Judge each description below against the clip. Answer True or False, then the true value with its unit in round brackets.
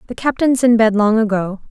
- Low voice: False (225 Hz)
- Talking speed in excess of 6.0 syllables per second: False (5.5 syllables/s)